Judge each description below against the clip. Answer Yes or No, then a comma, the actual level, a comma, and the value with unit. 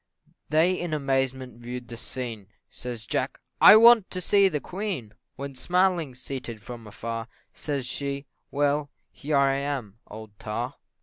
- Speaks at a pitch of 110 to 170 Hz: Yes, low, 135 Hz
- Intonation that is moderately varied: Yes, average, 4.4 semitones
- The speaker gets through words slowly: No, average, 145 wpm